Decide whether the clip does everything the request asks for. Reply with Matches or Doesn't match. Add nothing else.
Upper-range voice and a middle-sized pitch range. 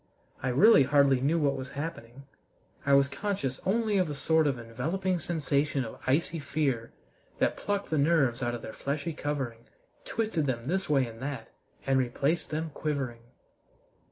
Doesn't match